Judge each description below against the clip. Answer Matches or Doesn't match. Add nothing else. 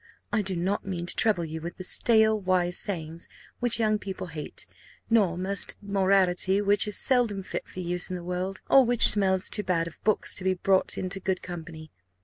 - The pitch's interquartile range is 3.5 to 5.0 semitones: Doesn't match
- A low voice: Doesn't match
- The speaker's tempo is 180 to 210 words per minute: Matches